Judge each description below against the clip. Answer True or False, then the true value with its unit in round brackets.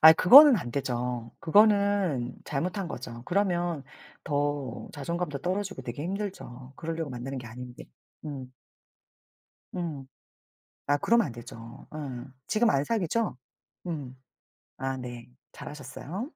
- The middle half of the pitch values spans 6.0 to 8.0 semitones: True (6.5 semitones)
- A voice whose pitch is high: False (145 Hz)